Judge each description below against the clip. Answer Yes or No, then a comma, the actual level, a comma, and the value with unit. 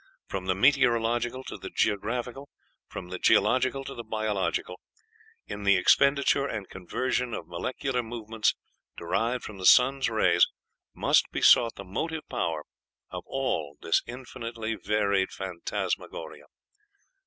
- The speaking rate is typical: No, slow, 130 wpm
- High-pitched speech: No, low, 115 Hz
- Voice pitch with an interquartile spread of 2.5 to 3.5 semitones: No, average, 4.7 semitones